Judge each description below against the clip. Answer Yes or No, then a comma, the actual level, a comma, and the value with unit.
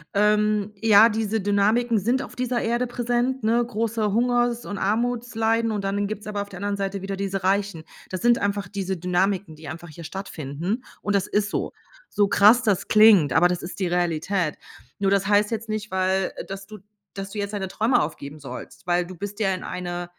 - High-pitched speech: Yes, high, 200 Hz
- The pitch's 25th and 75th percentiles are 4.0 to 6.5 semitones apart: No, average, 2.9 semitones